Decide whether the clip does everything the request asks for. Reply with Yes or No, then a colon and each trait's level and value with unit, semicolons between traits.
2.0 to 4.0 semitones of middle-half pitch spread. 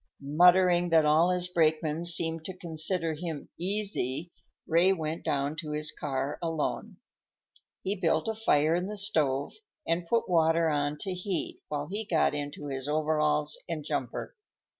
Yes: average, 3.0 semitones